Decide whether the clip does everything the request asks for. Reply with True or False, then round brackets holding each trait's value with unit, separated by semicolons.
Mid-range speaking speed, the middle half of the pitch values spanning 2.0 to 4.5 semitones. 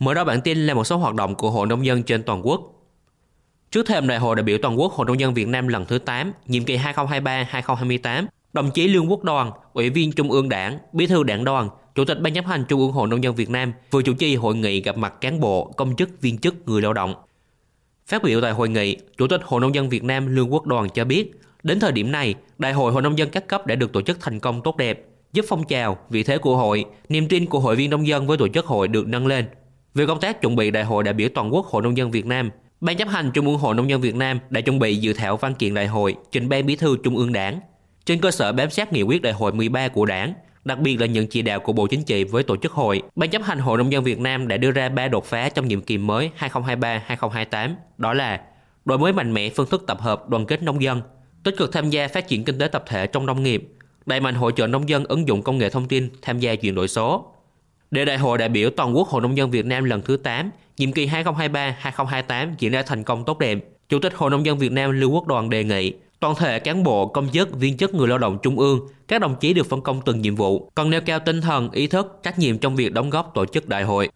False (275 wpm; 4.2 semitones)